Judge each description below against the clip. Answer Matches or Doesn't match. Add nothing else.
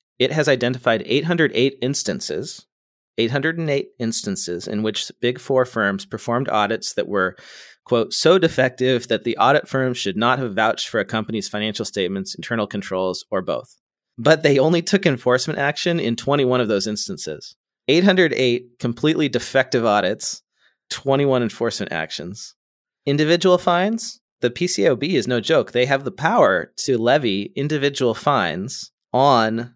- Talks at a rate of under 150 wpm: Matches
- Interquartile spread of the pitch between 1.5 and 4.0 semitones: Doesn't match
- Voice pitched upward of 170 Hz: Doesn't match